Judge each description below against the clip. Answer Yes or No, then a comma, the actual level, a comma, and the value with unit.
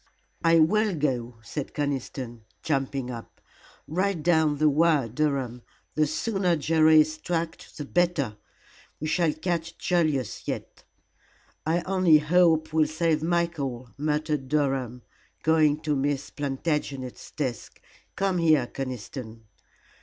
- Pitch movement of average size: Yes, average, 3.5 semitones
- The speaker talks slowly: Yes, slow, 120 wpm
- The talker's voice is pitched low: No, medium, 155 Hz